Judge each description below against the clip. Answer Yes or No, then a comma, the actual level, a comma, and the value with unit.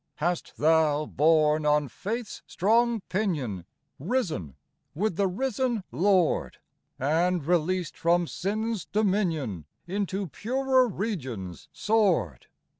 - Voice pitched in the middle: Yes, medium, 180 Hz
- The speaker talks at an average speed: No, slow, 100 wpm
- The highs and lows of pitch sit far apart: Yes, wide, 5.9 semitones